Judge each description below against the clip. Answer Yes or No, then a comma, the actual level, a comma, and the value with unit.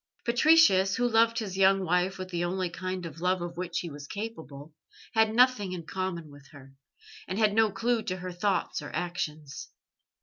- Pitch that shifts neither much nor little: Yes, average, 4.0 semitones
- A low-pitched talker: No, medium, 185 Hz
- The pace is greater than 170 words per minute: Yes, average, 190 wpm